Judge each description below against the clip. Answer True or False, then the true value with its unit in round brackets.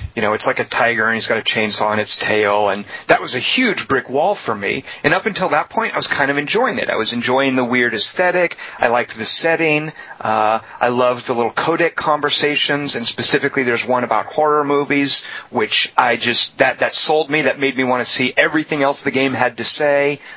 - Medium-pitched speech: False (130 Hz)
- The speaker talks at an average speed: False (240 wpm)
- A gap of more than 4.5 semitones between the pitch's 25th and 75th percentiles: False (4.2 semitones)